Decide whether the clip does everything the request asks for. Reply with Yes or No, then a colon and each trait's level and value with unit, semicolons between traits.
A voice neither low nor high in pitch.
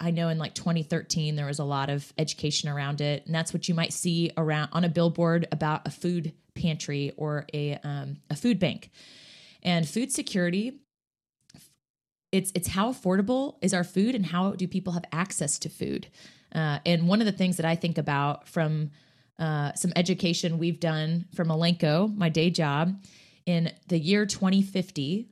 Yes: medium, 170 Hz